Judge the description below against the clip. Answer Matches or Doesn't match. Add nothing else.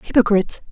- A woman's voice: Matches